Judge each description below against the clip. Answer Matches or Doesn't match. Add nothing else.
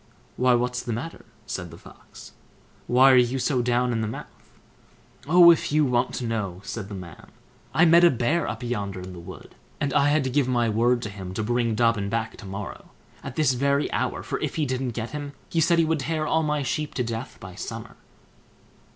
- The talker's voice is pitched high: Doesn't match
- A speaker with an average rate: Doesn't match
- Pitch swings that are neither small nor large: Matches